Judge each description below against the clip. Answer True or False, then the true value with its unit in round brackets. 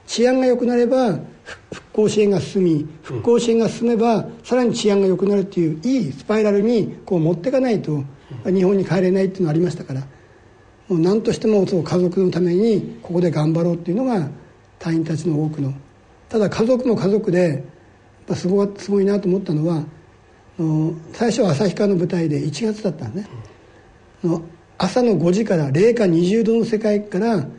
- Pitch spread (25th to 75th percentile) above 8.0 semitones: False (5.1 semitones)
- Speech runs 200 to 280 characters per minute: False (350 characters per minute)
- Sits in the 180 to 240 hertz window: True (185 Hz)